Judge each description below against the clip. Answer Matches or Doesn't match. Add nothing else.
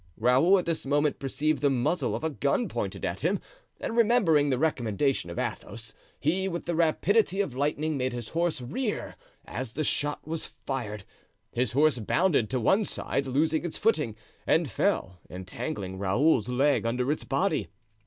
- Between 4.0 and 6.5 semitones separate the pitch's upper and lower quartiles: Matches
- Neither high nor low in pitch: Matches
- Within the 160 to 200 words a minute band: Matches